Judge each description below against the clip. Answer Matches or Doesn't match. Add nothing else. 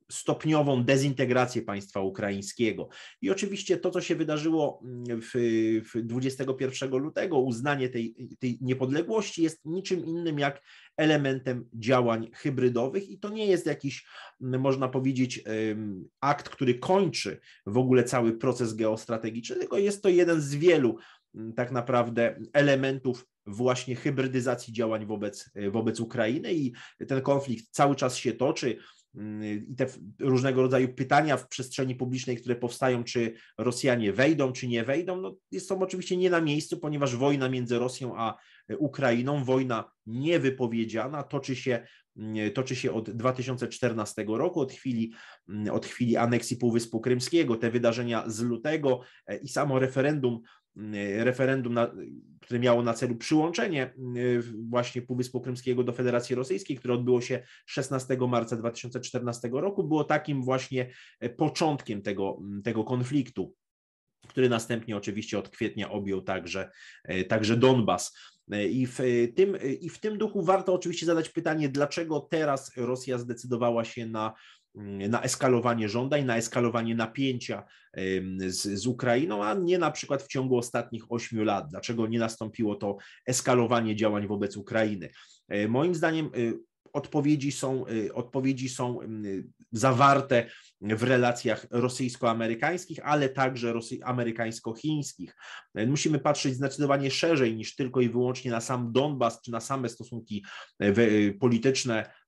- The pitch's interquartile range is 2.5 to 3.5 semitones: Matches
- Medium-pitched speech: Doesn't match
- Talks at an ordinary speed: Matches